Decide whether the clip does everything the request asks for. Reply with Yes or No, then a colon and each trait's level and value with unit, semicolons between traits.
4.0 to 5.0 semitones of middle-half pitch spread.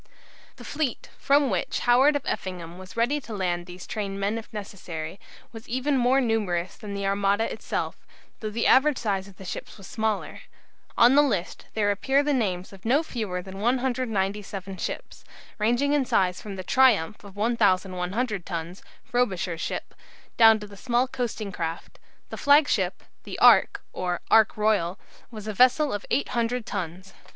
Yes: average, 4.5 semitones